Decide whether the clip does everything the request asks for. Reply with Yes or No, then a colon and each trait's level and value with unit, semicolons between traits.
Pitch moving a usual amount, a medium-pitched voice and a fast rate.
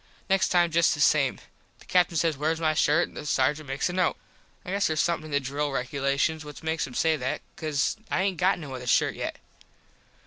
Yes: average, 3.3 semitones; medium, 155 Hz; fast, 220 wpm